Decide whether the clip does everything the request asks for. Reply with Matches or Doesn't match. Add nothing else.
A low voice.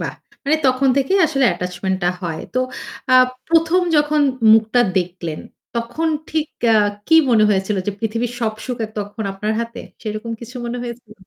Doesn't match